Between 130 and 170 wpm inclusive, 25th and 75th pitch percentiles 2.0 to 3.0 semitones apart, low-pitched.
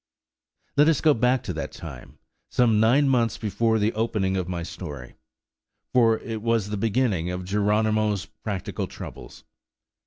No: average, 150 wpm; average, 3.4 semitones; low, 110 Hz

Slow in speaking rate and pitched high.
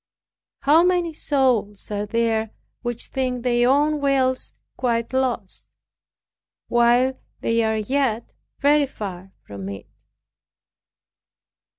Yes: slow, 100 wpm; high, 240 Hz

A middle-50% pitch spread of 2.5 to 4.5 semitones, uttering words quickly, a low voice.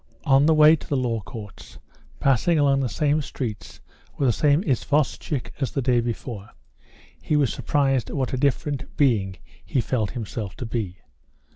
No: average, 4.0 semitones; average, 165 wpm; low, 130 Hz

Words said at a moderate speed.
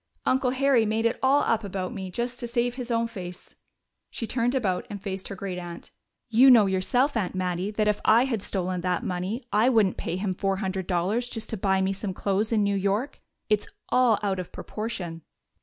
No: fast, 210 wpm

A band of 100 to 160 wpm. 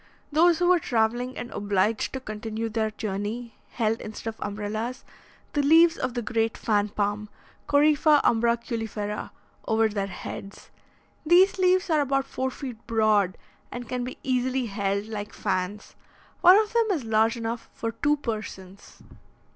Yes: average, 150 wpm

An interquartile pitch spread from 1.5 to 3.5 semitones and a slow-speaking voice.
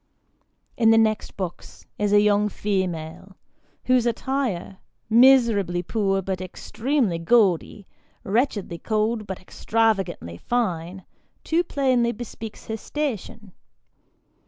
No: average, 3.9 semitones; slow, 105 wpm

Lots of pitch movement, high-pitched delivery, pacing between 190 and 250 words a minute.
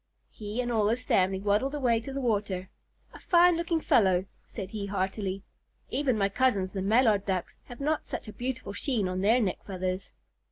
No: average, 4.8 semitones; high, 210 Hz; average, 195 wpm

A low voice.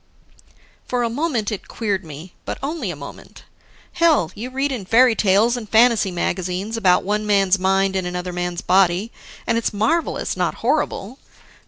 No: high, 205 Hz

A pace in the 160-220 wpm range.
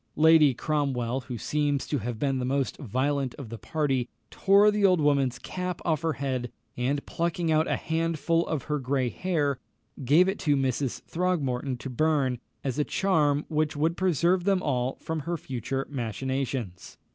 Yes: average, 170 wpm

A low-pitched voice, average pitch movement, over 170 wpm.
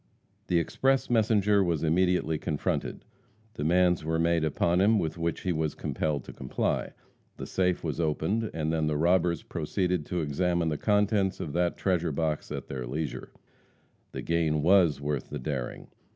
No: very low, 85 Hz; average, 3.0 semitones; average, 165 wpm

